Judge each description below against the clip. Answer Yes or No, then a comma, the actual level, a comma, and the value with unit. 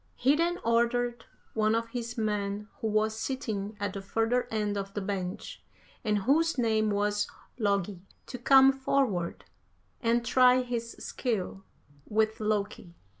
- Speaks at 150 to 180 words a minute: No, average, 140 wpm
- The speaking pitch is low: No, high, 220 Hz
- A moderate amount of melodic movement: Yes, average, 3.1 semitones